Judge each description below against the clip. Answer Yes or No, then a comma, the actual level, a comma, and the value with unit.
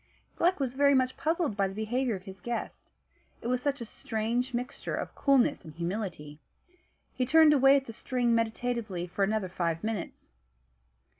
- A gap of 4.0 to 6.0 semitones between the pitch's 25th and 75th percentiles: Yes, average, 4.8 semitones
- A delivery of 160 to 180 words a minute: Yes, average, 170 wpm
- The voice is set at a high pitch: Yes, high, 235 Hz